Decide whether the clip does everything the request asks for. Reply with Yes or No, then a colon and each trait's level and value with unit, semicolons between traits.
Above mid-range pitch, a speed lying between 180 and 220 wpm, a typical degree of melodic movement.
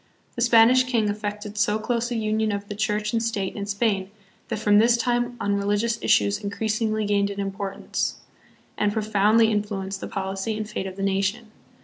No: high, 210 Hz; average, 185 wpm; narrow, 2.0 semitones